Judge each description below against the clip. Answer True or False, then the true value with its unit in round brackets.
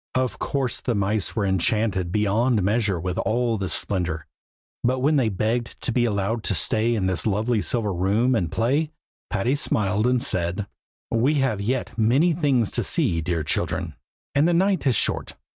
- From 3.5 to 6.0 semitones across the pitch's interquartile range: True (4.5 semitones)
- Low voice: True (110 Hz)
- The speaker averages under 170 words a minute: False (175 wpm)